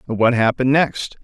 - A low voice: Yes, low, 125 Hz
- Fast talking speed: No, average, 145 wpm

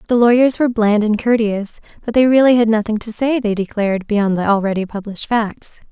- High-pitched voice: Yes, high, 220 Hz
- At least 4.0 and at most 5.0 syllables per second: No, 5.9 syllables/s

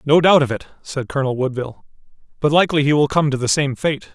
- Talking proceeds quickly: Yes, fast, 230 wpm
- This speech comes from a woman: No, male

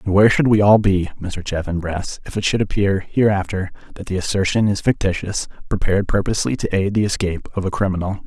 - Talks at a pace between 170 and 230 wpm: Yes, average, 190 wpm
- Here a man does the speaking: Yes, male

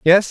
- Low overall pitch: No, medium, 185 Hz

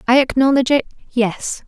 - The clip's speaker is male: No, female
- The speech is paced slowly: Yes, slow, 110 wpm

